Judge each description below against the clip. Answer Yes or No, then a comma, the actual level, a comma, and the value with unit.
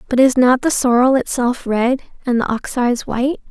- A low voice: No, very high, 250 Hz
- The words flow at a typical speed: Yes, average, 190 wpm